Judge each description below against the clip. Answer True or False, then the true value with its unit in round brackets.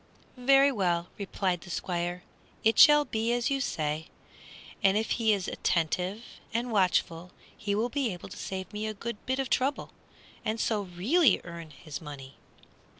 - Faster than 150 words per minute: True (165 wpm)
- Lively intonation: False (5.0 semitones)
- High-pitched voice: True (200 Hz)